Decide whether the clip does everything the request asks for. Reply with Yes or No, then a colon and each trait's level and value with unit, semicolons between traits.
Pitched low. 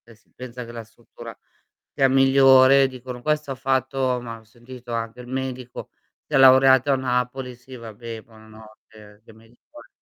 Yes: low, 125 Hz